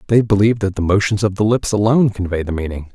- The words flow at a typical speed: No, fast, 245 wpm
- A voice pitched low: Yes, low, 100 Hz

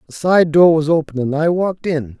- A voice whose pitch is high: No, medium, 160 Hz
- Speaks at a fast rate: Yes, fast, 245 wpm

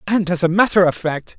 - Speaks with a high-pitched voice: No, medium, 180 Hz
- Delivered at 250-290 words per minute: Yes, fast, 260 wpm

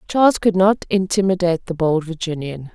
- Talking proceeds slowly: No, average, 155 wpm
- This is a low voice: No, medium, 180 Hz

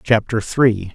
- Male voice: Yes, male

